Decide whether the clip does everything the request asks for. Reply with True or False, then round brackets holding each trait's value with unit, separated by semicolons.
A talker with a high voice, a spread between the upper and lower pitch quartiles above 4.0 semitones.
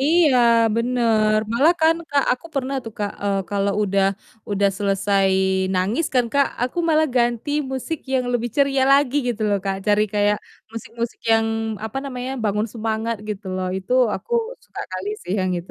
True (230 Hz; 4.7 semitones)